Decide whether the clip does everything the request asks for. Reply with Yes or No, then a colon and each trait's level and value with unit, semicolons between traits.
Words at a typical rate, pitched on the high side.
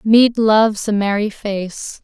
Yes: average, 150 wpm; high, 210 Hz